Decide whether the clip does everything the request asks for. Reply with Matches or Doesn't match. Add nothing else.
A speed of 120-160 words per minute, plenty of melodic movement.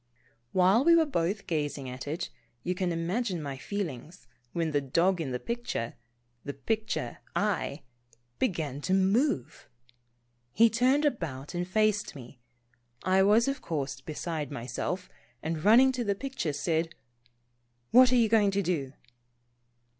Matches